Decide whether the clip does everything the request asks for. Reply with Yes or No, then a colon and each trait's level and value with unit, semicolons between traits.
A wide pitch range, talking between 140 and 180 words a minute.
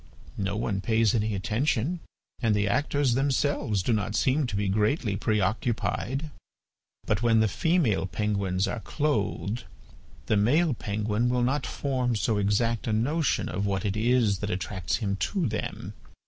No: average, 3.8 semitones; average, 155 wpm